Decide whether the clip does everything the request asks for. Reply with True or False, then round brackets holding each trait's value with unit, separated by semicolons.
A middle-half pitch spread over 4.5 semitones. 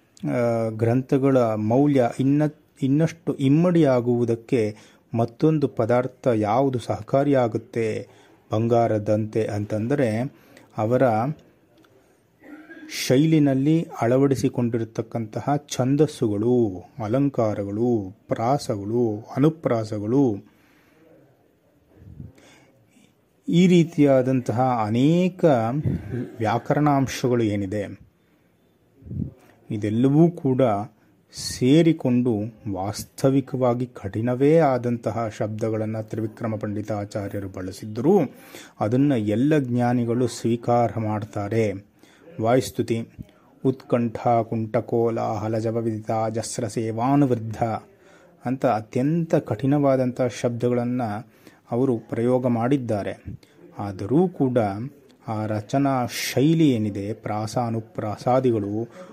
False (3.7 semitones)